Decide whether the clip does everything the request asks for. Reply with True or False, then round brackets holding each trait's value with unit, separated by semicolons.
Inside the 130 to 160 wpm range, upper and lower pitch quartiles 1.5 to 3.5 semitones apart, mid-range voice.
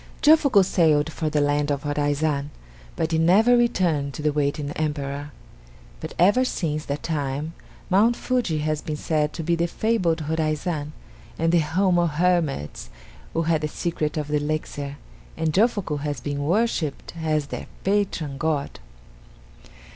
True (155 wpm; 2.9 semitones; 155 Hz)